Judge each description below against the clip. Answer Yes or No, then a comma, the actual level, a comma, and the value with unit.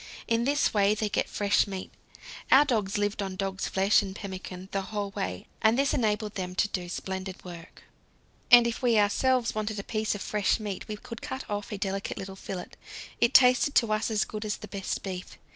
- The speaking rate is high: Yes, fast, 210 wpm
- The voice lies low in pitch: No, high, 205 Hz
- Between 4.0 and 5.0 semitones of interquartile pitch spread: No, narrow, 2.4 semitones